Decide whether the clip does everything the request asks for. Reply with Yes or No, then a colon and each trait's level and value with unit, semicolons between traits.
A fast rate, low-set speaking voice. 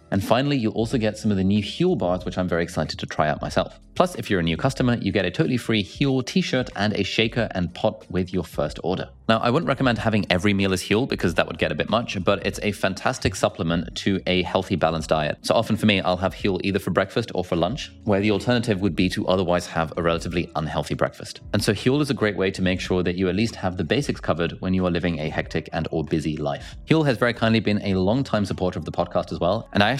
Yes: fast, 270 wpm; low, 100 Hz